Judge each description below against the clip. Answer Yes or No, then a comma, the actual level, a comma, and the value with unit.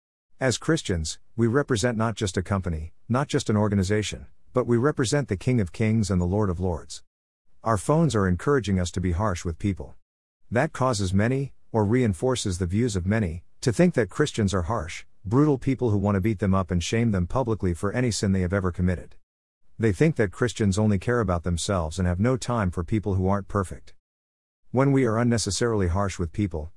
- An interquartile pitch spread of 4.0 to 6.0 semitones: Yes, average, 4.9 semitones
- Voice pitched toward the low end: Yes, low, 105 Hz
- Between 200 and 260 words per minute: Yes, fast, 205 wpm